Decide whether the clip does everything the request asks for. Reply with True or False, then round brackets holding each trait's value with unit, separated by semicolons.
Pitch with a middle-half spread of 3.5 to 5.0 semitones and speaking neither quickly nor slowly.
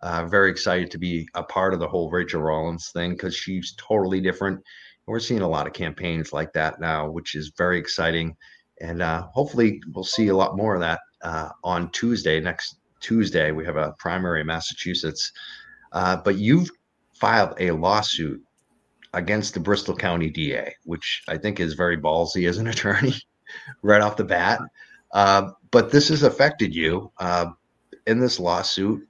True (3.8 semitones; 175 wpm)